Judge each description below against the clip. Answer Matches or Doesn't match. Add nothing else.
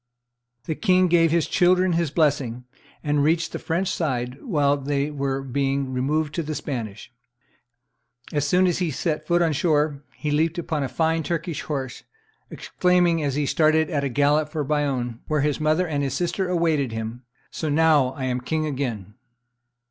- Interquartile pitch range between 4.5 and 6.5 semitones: Doesn't match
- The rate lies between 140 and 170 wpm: Doesn't match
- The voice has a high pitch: Doesn't match